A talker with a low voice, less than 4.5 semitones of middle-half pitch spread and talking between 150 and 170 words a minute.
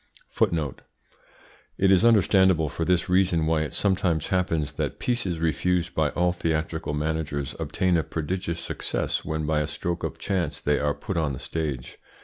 Yes: very low, 80 Hz; average, 2.9 semitones; average, 160 wpm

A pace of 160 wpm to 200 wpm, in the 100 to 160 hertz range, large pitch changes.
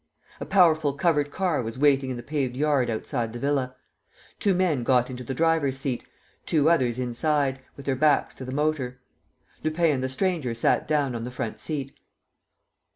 No: average, 180 wpm; medium, 140 Hz; average, 3.4 semitones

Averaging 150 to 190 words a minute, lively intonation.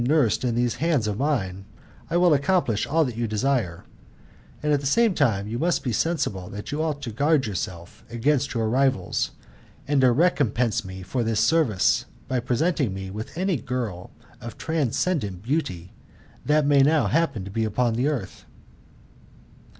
Yes: average, 165 wpm; wide, 5.8 semitones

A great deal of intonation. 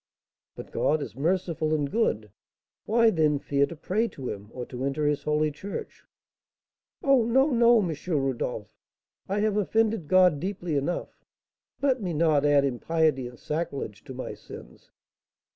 Yes: wide, 6.3 semitones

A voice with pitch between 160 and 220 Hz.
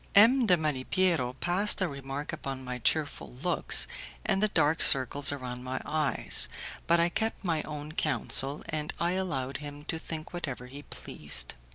No: medium, 150 Hz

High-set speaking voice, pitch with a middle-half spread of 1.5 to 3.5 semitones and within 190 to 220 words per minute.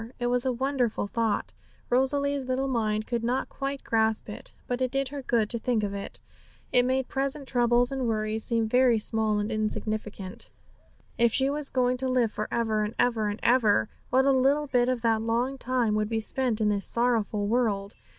Yes: high, 240 Hz; average, 3.1 semitones; average, 200 wpm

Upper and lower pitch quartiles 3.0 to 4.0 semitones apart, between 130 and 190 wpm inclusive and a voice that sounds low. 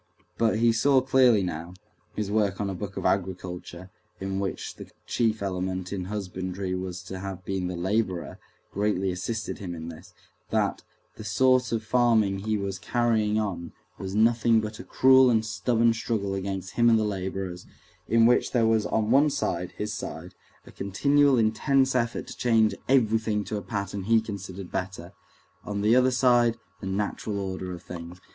Yes: average, 3.4 semitones; average, 170 wpm; low, 105 Hz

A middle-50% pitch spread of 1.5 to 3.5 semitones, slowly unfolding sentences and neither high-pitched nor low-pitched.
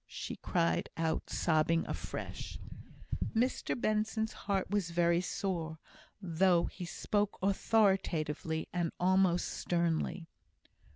Yes: average, 3.0 semitones; slow, 100 wpm; medium, 175 Hz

